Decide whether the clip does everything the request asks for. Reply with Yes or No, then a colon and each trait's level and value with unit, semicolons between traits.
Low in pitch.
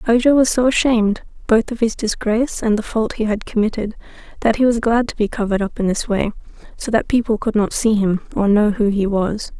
No: high, 220 Hz